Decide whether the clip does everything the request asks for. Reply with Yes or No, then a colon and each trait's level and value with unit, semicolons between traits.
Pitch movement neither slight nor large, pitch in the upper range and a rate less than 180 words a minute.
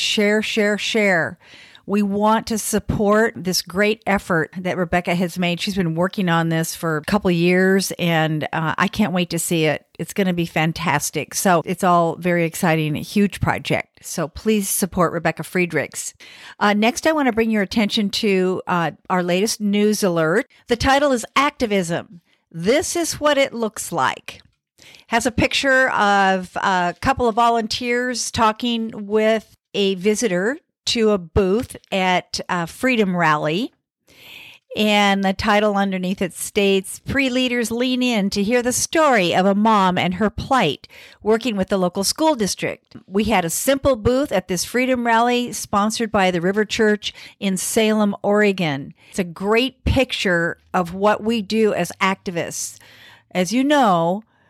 Yes: average, 4.0 semitones; high, 200 Hz; average, 165 wpm